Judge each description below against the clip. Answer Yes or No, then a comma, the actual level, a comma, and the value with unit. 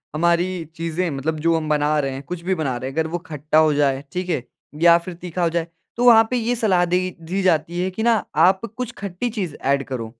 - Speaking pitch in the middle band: Yes, medium, 170 Hz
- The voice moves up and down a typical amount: Yes, average, 3.4 semitones